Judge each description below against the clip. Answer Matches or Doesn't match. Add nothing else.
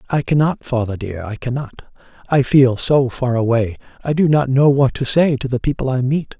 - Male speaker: Matches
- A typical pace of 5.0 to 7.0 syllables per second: Matches